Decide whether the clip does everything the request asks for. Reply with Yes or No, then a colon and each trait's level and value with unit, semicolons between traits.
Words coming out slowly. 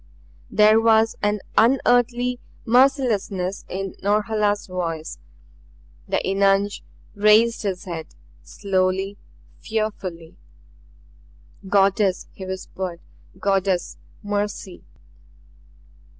Yes: slow, 75 wpm